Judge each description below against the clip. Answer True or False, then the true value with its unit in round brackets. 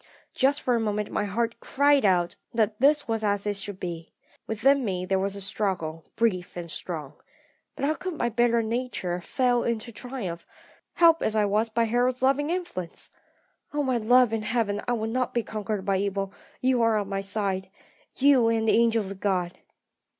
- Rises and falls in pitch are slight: False (3.9 semitones)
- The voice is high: True (220 Hz)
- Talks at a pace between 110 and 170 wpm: False (190 wpm)